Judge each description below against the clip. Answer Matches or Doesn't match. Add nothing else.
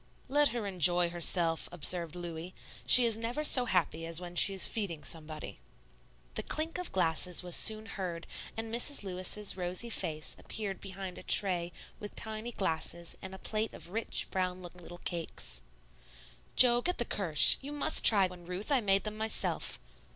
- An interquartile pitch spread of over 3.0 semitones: Matches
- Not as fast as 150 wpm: Doesn't match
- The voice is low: Doesn't match